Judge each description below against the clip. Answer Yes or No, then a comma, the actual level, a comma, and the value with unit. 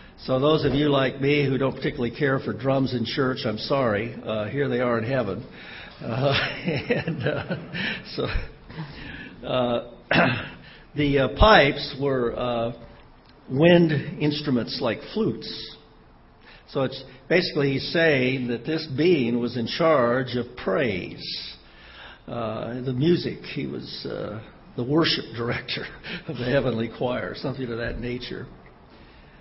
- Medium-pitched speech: No, low, 130 Hz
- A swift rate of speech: No, slow, 135 wpm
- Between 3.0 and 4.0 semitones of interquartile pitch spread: Yes, average, 3.3 semitones